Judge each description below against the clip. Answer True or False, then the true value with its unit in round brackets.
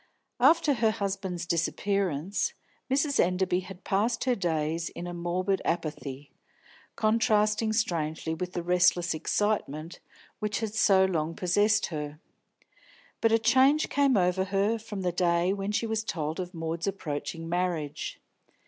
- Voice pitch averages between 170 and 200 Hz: True (185 Hz)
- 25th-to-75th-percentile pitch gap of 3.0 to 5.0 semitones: True (4.2 semitones)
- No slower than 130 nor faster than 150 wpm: True (140 wpm)